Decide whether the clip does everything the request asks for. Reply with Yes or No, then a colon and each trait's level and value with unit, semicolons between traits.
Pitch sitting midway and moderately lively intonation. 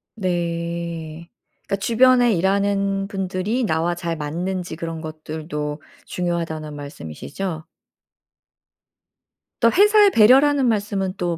Yes: medium, 175 Hz; average, 4.0 semitones